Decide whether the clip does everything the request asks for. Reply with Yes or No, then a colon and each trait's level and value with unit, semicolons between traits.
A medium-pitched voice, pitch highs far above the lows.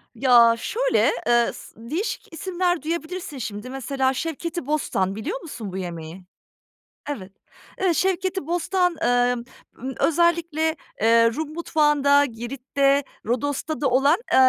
No: very high, 285 Hz; wide, 5.9 semitones